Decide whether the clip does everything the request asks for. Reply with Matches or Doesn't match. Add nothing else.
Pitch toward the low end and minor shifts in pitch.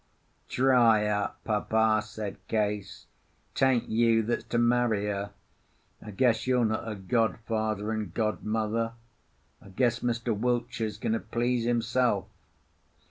Matches